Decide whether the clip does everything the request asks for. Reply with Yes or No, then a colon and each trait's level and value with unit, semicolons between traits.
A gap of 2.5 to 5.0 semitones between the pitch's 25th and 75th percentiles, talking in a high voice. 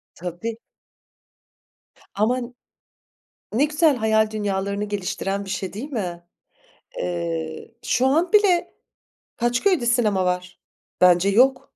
No: wide, 5.5 semitones; high, 215 Hz